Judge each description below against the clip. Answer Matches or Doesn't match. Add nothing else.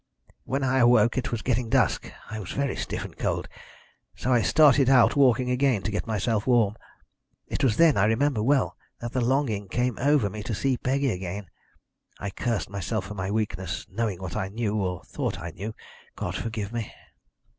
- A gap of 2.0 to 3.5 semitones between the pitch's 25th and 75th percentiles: Doesn't match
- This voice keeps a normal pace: Matches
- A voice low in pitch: Matches